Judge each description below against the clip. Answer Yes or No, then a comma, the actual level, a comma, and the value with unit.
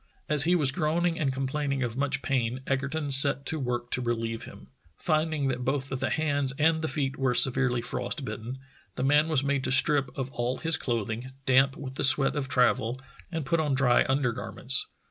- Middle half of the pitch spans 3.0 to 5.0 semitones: No, narrow, 2.6 semitones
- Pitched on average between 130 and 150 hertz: Yes, low, 135 Hz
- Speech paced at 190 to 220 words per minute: Yes, average, 195 wpm